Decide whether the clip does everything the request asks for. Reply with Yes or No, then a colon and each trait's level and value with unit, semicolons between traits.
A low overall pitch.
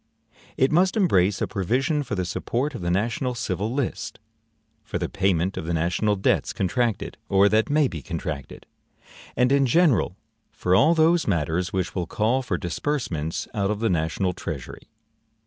Yes: low, 105 Hz